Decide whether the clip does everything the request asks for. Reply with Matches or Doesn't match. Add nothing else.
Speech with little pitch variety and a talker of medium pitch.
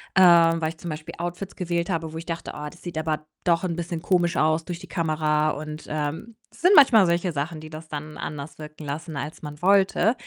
Matches